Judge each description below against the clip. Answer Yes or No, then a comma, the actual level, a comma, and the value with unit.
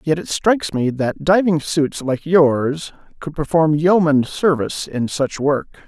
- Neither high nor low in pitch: Yes, medium, 155 Hz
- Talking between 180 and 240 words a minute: No, average, 165 wpm